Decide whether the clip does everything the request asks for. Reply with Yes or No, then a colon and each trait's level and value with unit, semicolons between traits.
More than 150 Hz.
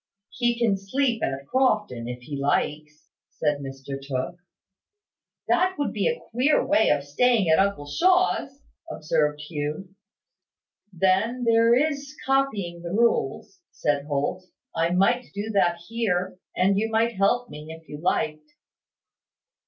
Yes: high, 190 Hz